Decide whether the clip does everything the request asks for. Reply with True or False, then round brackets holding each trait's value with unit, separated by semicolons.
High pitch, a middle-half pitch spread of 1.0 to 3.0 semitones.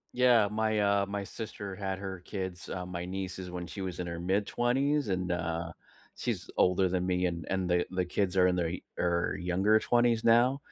False (95 Hz; 2.7 semitones)